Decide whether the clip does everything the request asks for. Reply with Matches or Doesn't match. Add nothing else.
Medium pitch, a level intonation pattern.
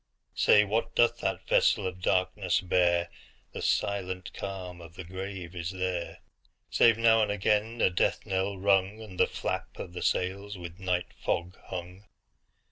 Doesn't match